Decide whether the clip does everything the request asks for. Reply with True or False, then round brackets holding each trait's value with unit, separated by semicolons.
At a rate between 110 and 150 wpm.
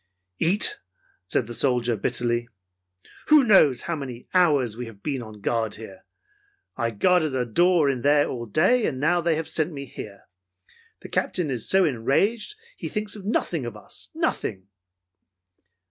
False (160 wpm)